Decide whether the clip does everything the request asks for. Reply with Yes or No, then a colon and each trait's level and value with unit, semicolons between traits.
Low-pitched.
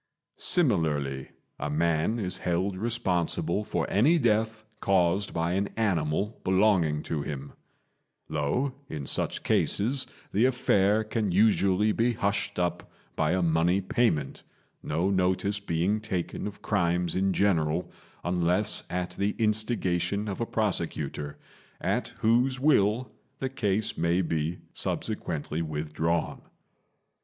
Yes: very low, 95 Hz